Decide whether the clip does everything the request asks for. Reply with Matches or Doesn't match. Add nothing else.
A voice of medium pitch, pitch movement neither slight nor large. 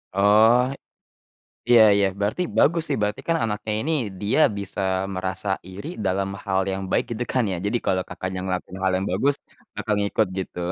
Doesn't match